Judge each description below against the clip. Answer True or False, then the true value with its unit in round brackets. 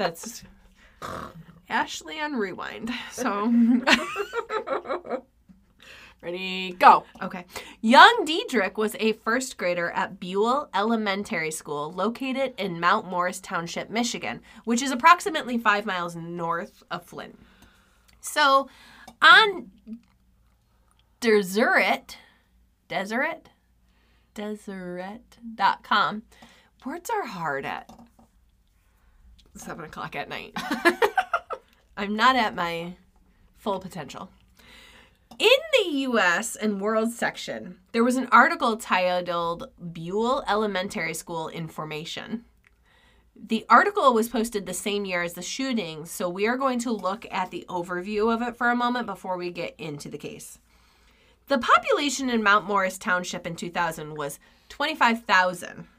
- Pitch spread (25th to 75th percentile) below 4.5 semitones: False (5.3 semitones)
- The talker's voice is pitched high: True (210 Hz)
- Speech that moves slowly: True (115 wpm)